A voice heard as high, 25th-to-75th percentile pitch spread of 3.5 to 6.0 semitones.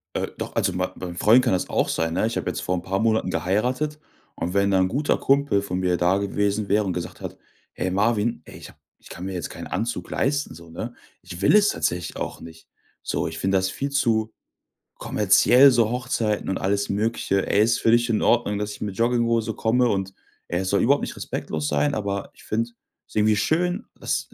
No: low, 105 Hz; average, 4.1 semitones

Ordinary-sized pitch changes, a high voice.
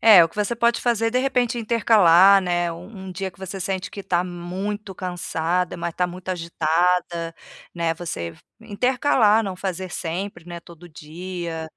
No: average, 3.1 semitones; medium, 180 Hz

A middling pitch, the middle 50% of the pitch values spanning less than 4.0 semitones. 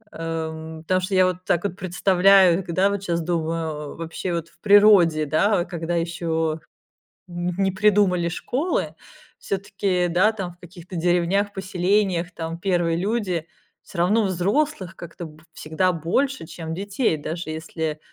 Yes: medium, 175 Hz; average, 2.8 semitones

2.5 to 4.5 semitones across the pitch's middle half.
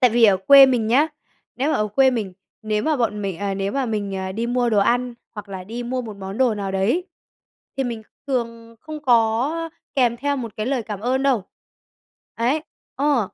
Yes: average, 3.9 semitones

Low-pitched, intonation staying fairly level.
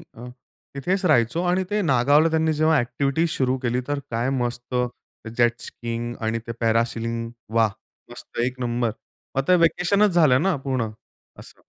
No: low, 130 Hz; average, 5.1 semitones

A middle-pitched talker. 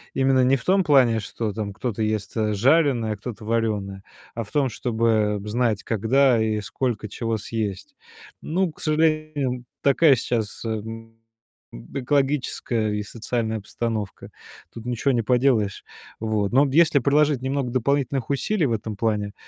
No: low, 115 Hz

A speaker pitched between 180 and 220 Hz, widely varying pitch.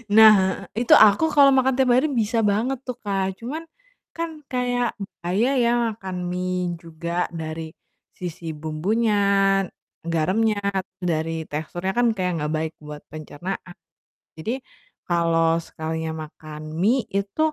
Yes: high, 190 Hz; wide, 6.3 semitones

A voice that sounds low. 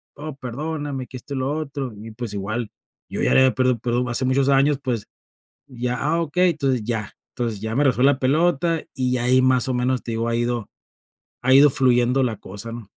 Yes: low, 130 Hz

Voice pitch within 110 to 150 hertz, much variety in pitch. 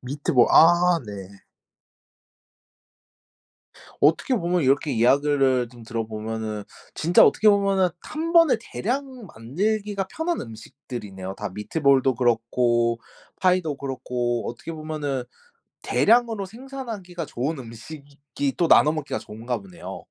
Yes: medium, 140 Hz; wide, 7.7 semitones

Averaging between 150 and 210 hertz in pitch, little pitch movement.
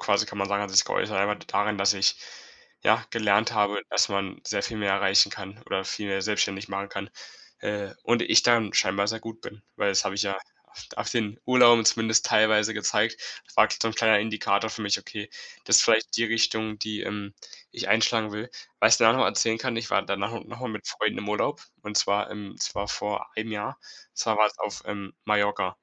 No: low, 105 Hz; narrow, 1.9 semitones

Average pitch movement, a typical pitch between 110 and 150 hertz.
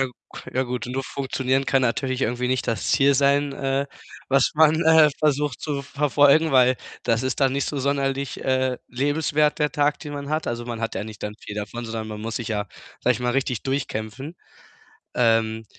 Yes: average, 3.1 semitones; low, 135 Hz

